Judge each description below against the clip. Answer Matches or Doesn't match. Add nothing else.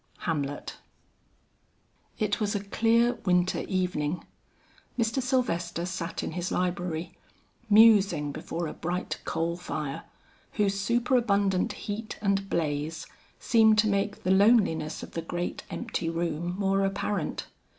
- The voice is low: Doesn't match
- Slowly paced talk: Matches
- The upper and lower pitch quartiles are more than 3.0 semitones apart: Matches